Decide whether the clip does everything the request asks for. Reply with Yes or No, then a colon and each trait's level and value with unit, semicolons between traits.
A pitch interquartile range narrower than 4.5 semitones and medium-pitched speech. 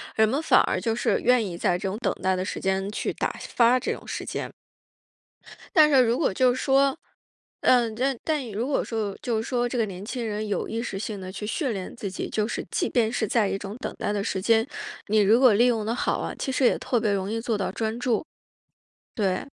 No: average, 3.4 semitones; high, 225 Hz